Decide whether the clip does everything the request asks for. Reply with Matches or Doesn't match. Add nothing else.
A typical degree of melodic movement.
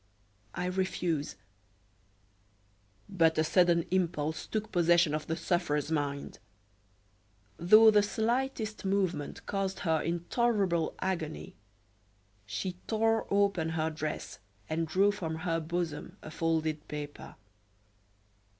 Matches